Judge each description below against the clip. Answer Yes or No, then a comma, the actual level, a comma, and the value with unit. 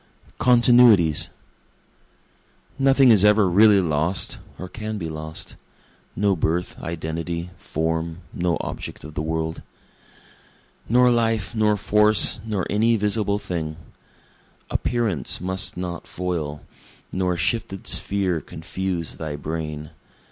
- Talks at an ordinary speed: No, slow, 110 wpm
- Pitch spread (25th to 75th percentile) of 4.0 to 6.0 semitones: Yes, average, 4.7 semitones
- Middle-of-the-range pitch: No, very low, 90 Hz